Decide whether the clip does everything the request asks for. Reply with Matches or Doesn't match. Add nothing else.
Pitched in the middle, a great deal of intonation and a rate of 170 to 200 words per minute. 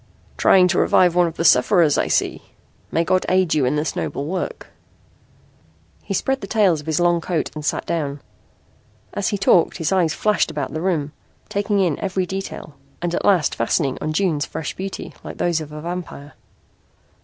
Doesn't match